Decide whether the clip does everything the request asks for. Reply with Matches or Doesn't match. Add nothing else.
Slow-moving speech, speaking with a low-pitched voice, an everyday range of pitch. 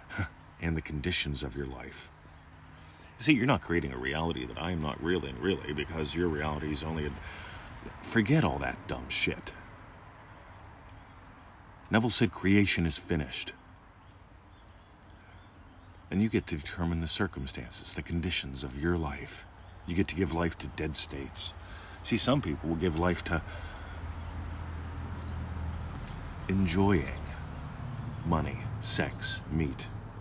Matches